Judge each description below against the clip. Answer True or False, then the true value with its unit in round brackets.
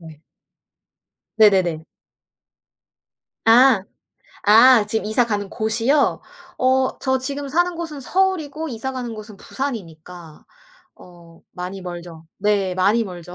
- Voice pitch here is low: False (220 Hz)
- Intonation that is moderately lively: False (6.6 semitones)